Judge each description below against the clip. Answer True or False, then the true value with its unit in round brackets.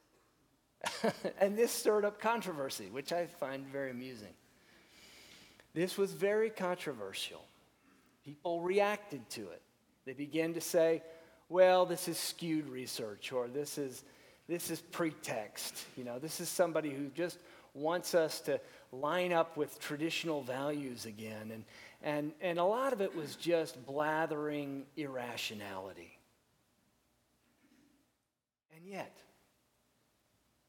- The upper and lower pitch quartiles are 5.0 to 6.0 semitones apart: False (4.4 semitones)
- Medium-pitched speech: True (160 Hz)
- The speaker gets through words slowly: True (120 wpm)